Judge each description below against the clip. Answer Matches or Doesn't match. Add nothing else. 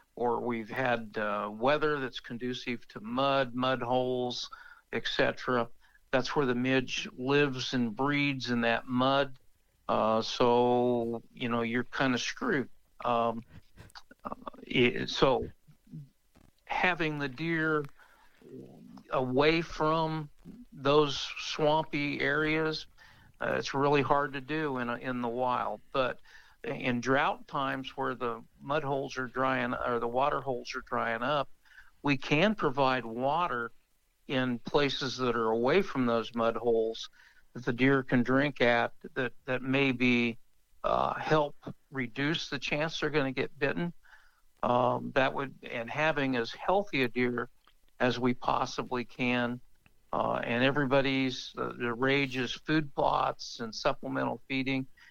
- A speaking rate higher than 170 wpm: Doesn't match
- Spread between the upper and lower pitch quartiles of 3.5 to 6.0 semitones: Doesn't match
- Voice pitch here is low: Matches